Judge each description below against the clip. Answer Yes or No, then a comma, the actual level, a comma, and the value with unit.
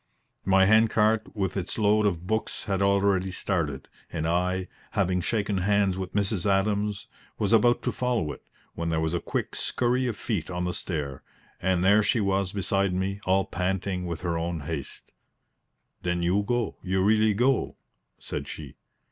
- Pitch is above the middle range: No, very low, 95 Hz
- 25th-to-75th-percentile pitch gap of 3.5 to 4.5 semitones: No, average, 2.7 semitones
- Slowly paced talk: No, average, 175 wpm